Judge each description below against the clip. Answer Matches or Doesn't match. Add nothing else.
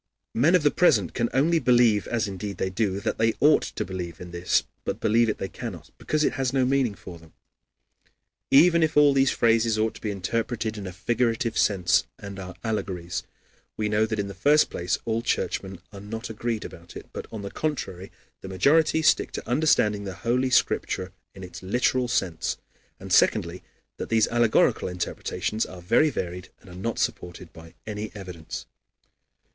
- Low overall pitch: Matches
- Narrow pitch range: Doesn't match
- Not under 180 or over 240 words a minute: Matches